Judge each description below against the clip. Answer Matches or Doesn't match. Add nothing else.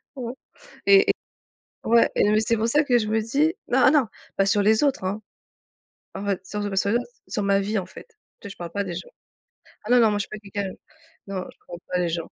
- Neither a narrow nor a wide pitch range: Matches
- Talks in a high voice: Matches